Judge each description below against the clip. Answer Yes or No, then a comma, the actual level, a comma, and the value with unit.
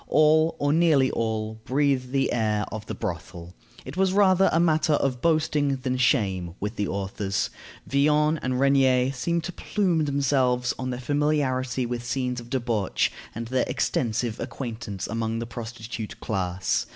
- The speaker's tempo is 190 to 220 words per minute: No, average, 160 wpm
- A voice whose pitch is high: No, low, 125 Hz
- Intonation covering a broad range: No, average, 4.4 semitones